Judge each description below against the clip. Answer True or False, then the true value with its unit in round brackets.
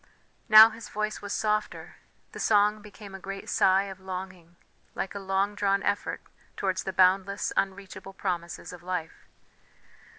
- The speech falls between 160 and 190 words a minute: False (145 wpm)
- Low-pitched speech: False (195 Hz)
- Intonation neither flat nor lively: False (1.6 semitones)